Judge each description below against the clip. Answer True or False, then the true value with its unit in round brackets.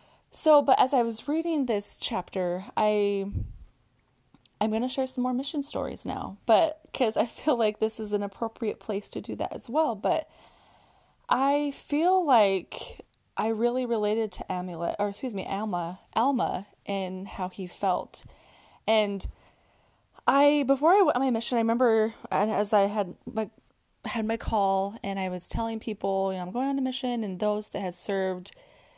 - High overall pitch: True (220 Hz)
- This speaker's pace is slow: False (175 wpm)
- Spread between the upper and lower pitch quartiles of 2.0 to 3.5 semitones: False (4.5 semitones)